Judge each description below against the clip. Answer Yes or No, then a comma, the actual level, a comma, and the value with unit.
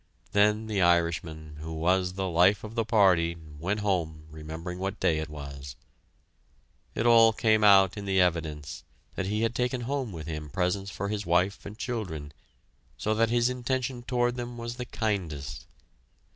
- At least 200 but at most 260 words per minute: No, average, 170 wpm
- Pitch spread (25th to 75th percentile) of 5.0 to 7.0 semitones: Yes, wide, 5.5 semitones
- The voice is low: Yes, very low, 95 Hz